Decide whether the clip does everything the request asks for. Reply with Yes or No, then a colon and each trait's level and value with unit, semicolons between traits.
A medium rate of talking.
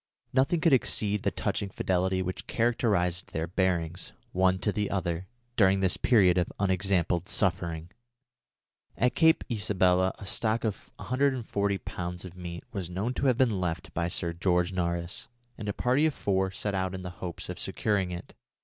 Yes: average, 170 wpm